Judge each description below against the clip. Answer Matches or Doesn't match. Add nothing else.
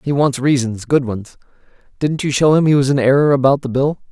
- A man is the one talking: Matches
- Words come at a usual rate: Doesn't match